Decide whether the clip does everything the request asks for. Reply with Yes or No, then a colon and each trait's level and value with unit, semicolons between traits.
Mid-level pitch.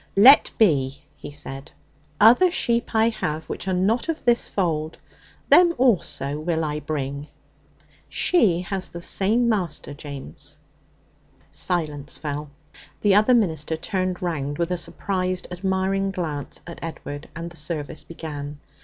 Yes: medium, 170 Hz